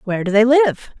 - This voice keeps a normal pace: No, fast, 240 wpm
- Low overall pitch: No, high, 235 Hz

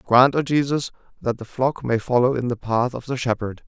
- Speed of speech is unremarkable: No, fast, 230 wpm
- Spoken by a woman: No, male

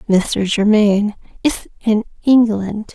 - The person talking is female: Yes, female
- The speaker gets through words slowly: Yes, slow, 100 wpm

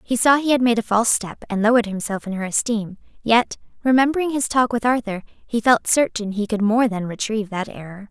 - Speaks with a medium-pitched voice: No, high, 225 Hz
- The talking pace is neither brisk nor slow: No, fast, 220 wpm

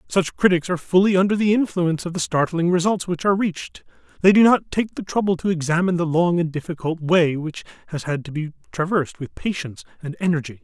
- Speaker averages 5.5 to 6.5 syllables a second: Yes, 6.3 syllables/s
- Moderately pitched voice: Yes, medium, 170 Hz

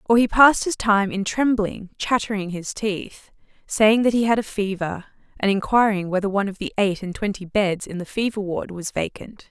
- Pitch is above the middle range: Yes, high, 205 Hz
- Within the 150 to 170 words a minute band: No, average, 200 wpm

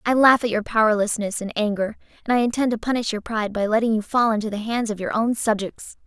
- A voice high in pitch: Yes, high, 220 Hz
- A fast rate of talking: Yes, fast, 245 wpm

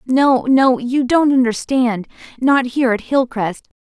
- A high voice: Yes, very high, 250 Hz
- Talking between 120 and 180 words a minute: Yes, average, 140 wpm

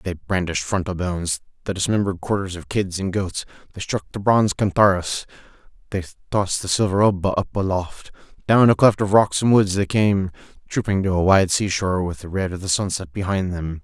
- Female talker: No, male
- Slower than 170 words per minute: No, average, 195 wpm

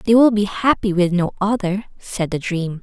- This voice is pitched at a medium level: No, high, 195 Hz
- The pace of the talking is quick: Yes, fast, 210 wpm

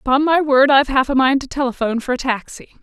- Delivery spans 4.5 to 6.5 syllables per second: No, 6.7 syllables/s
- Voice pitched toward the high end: Yes, very high, 265 Hz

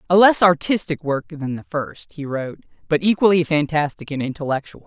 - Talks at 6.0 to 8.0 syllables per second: No, 5.5 syllables/s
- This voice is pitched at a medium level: Yes, medium, 160 Hz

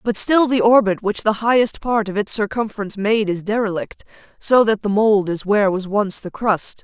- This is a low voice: No, high, 210 Hz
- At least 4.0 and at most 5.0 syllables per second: No, 5.2 syllables/s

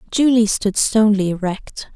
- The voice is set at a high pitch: Yes, high, 210 Hz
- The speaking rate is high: No, slow, 125 wpm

